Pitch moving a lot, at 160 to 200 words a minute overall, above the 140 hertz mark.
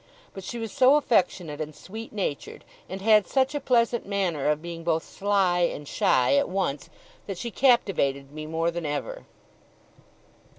Yes: wide, 6.4 semitones; average, 165 wpm; medium, 185 Hz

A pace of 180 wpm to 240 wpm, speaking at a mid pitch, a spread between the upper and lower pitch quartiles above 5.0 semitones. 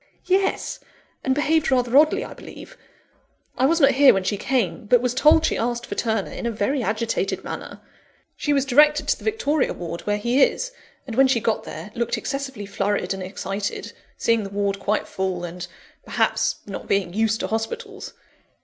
No: average, 185 wpm; high, 235 Hz; wide, 5.5 semitones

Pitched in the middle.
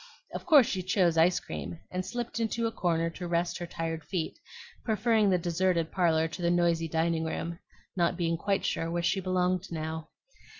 Yes: medium, 175 Hz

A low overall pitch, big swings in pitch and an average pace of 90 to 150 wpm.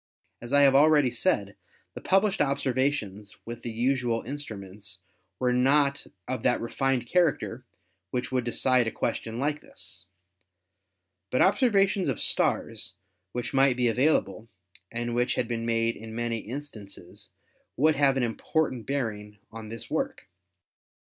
No: low, 125 Hz; average, 3.7 semitones; average, 140 wpm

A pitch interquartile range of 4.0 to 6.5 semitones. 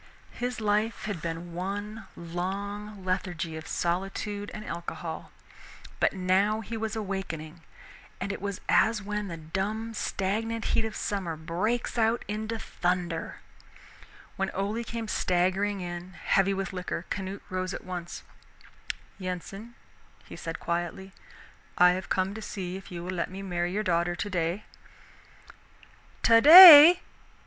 No: average, 3.2 semitones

